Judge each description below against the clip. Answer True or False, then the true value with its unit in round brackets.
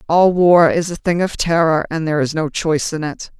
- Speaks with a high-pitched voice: False (160 Hz)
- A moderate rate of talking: False (245 wpm)